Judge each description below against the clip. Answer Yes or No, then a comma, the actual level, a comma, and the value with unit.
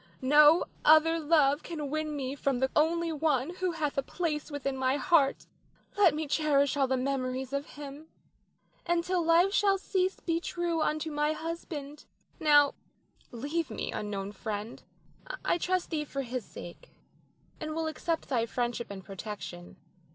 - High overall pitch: Yes, very high, 295 Hz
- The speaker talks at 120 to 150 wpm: No, average, 160 wpm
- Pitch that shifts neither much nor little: Yes, average, 3.7 semitones